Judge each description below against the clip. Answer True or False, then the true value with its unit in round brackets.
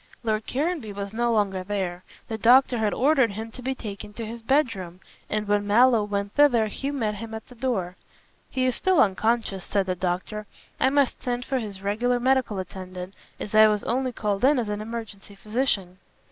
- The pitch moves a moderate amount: True (3.6 semitones)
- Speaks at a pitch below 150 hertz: False (220 Hz)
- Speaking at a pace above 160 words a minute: True (195 wpm)